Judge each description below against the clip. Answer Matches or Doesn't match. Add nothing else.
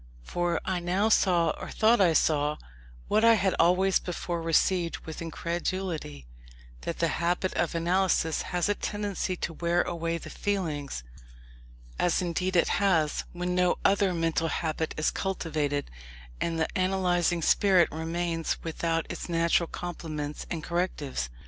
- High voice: Doesn't match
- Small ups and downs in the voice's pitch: Matches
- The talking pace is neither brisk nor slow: Matches